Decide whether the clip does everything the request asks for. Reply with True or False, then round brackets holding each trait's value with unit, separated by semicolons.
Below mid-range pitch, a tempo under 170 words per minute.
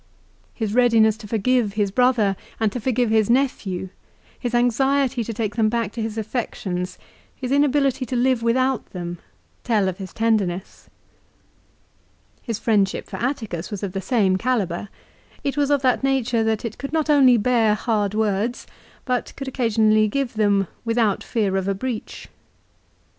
False (225 Hz; 160 wpm)